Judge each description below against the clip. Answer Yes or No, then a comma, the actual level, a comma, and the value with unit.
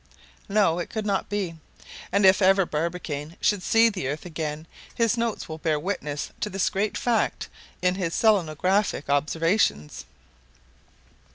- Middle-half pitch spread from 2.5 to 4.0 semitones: No, average, 4.6 semitones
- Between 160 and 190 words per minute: No, average, 145 wpm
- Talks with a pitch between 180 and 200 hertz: Yes, medium, 185 Hz